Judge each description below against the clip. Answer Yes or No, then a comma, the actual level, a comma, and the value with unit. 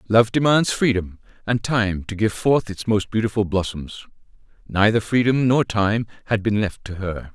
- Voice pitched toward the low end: Yes, low, 110 Hz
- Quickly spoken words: No, average, 170 wpm